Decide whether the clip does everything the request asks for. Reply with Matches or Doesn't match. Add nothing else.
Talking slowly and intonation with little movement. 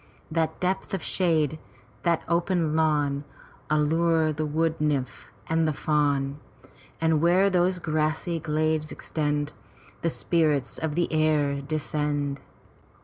Matches